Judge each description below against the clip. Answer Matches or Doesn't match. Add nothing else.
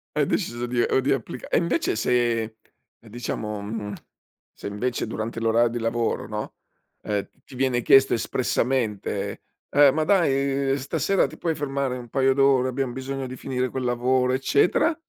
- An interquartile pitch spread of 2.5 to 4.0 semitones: Matches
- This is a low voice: Matches